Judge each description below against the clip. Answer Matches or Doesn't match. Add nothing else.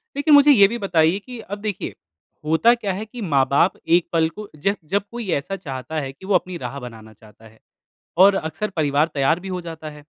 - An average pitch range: Doesn't match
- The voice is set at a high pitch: Doesn't match